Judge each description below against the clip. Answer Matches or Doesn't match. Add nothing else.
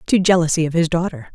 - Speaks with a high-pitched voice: Doesn't match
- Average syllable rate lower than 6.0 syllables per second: Doesn't match